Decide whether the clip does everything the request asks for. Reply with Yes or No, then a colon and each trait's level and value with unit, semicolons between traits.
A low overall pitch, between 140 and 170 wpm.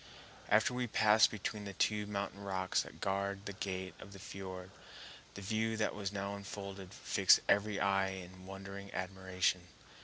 Yes: low, 100 Hz; average, 155 wpm